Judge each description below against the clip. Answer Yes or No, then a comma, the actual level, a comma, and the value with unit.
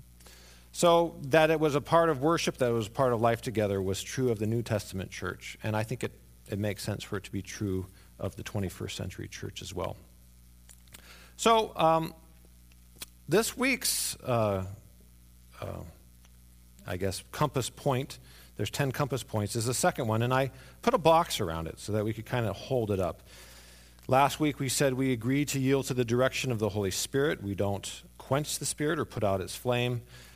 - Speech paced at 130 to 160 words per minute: No, average, 200 wpm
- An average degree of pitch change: No, wide, 7.6 semitones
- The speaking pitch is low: Yes, low, 105 Hz